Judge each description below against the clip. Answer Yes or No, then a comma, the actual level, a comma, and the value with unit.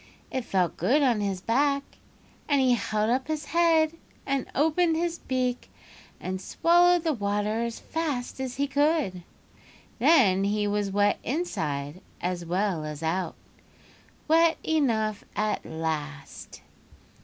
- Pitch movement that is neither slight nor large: No, wide, 7.9 semitones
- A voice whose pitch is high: Yes, high, 235 Hz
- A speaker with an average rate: No, slow, 130 wpm